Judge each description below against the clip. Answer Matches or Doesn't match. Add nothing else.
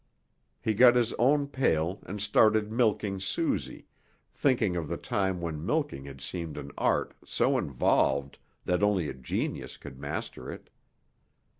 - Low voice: Matches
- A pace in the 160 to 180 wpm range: Doesn't match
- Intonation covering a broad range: Matches